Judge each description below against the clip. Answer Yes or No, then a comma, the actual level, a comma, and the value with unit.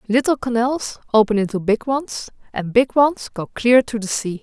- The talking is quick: No, average, 190 wpm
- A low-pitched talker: No, high, 235 Hz